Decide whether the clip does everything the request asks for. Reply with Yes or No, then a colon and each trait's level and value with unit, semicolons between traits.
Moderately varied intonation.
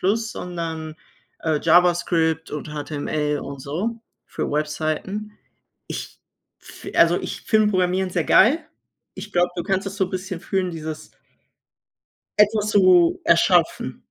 Yes: average, 3.9 semitones